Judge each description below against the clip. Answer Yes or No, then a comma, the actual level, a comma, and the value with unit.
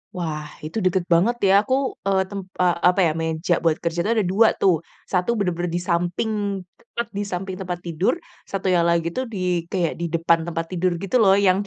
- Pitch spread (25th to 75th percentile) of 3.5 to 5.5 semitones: No, narrow, 2.5 semitones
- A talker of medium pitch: Yes, medium, 180 Hz